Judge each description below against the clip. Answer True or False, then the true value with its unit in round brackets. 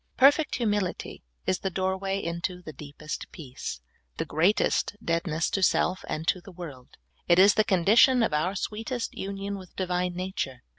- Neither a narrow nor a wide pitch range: True (3.0 semitones)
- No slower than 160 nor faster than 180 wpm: True (170 wpm)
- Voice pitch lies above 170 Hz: True (185 Hz)